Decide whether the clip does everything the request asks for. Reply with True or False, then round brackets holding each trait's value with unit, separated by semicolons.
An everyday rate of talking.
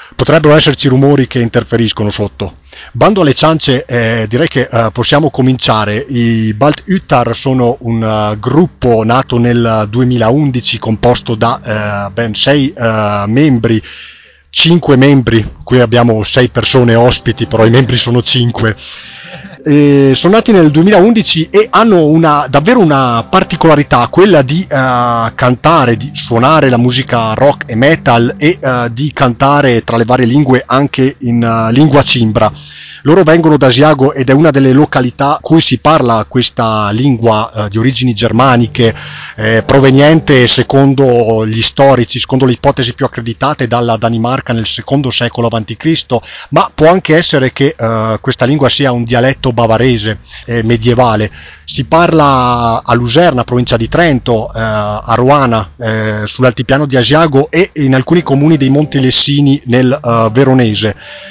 True (150 wpm)